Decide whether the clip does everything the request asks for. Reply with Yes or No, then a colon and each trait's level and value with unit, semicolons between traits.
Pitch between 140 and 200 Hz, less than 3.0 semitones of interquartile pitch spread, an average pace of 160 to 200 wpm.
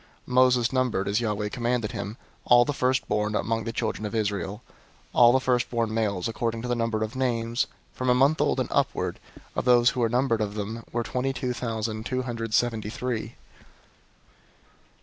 No: low, 115 Hz; narrow, 2.4 semitones; average, 190 wpm